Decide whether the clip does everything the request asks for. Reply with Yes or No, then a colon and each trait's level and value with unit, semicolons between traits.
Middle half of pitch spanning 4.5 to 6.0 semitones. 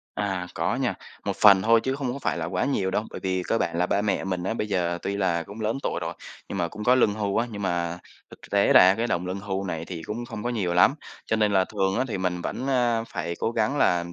No: average, 4.1 semitones